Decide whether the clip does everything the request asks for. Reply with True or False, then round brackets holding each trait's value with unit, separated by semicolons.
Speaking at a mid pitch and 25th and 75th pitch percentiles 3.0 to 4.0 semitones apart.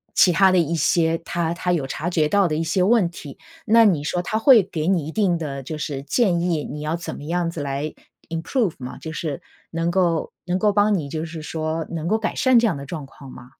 True (165 Hz; 3.3 semitones)